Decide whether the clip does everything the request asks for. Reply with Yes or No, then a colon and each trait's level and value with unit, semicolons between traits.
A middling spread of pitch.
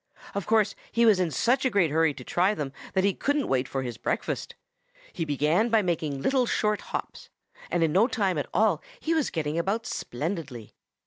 No: wide, 6.6 semitones